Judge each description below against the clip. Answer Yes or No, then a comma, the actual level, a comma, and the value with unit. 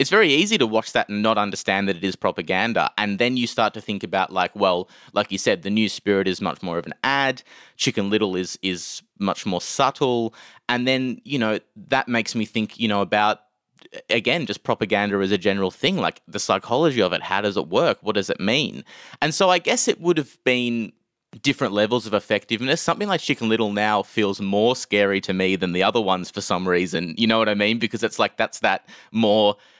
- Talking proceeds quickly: Yes, fast, 225 wpm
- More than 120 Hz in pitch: No, low, 105 Hz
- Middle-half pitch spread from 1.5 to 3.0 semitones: No, average, 3.6 semitones